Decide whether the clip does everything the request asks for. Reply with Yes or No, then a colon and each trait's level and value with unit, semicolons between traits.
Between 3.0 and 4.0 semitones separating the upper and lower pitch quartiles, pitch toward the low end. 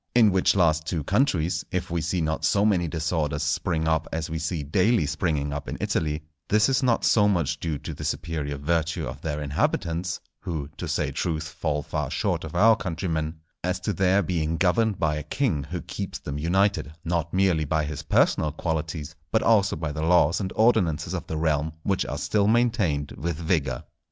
Yes: average, 3.5 semitones; very low, 80 Hz